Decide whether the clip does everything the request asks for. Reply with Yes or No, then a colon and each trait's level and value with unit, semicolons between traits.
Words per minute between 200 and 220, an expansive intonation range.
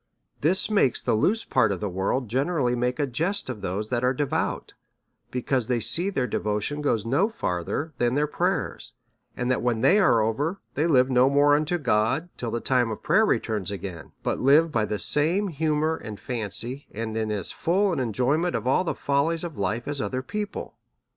Yes: fast, 205 wpm; wide, 5.7 semitones